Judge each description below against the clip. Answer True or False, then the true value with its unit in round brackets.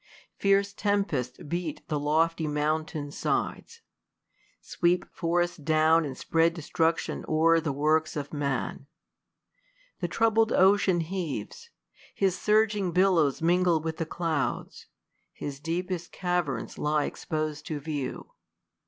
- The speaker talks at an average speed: False (115 wpm)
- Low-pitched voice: False (165 Hz)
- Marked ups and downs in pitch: False (3.0 semitones)